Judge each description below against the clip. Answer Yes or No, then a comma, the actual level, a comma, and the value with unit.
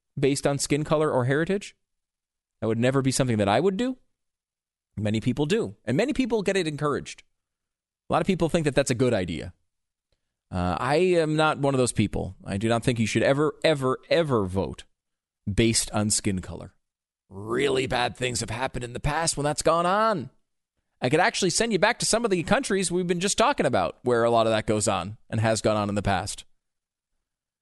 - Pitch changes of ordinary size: No, wide, 7.1 semitones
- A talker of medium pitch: No, low, 125 Hz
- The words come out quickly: Yes, fast, 215 wpm